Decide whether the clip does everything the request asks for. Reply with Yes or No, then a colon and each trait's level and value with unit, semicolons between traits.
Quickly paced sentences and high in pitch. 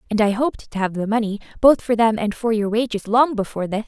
Yes: fast, 265 wpm; high, 220 Hz